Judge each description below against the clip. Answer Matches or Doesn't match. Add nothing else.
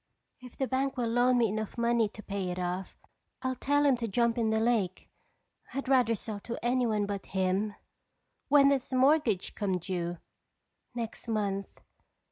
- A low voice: Doesn't match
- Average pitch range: Matches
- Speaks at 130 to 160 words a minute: Doesn't match